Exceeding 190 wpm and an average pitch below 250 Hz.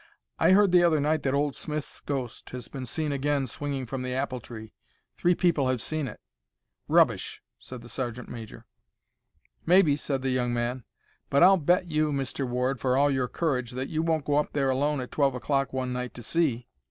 Yes: average, 200 wpm; low, 135 Hz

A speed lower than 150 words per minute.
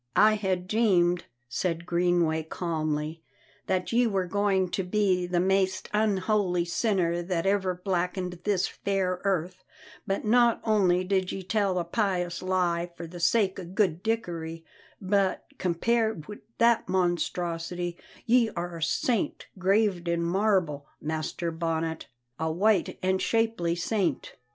Yes: slow, 135 wpm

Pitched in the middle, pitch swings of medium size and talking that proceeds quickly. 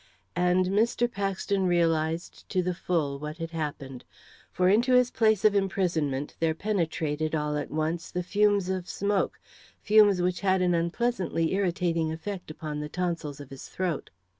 No: medium, 175 Hz; average, 3.7 semitones; average, 165 wpm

